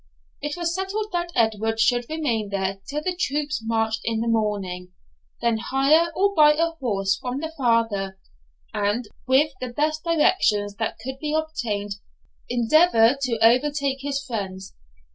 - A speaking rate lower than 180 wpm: Yes, average, 150 wpm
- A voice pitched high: Yes, high, 245 Hz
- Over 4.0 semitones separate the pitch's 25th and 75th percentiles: Yes, wide, 5.6 semitones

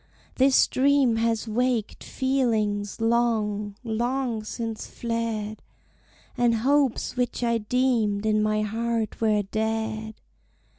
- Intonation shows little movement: Yes, narrow, 2.2 semitones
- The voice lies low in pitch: No, high, 225 Hz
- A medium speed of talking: No, slow, 105 wpm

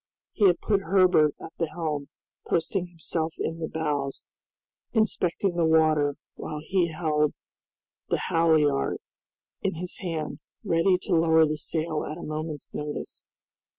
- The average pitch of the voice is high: No, medium, 160 Hz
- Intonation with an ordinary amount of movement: No, narrow, 2.2 semitones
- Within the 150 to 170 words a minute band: No, average, 140 wpm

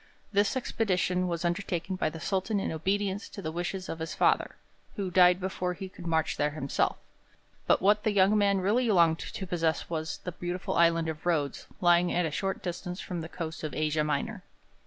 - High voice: No, medium, 180 Hz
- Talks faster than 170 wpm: Yes, average, 200 wpm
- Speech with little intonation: No, average, 3.0 semitones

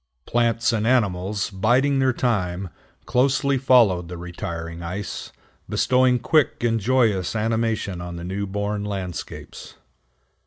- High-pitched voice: No, low, 105 Hz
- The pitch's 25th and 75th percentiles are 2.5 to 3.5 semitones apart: No, average, 5.1 semitones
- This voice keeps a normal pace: No, slow, 120 wpm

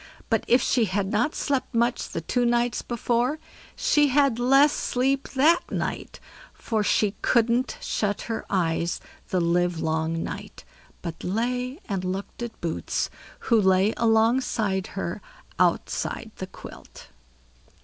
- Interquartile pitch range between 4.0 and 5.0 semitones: Yes, average, 4.7 semitones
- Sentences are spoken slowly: Yes, slow, 130 wpm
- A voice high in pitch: Yes, high, 225 Hz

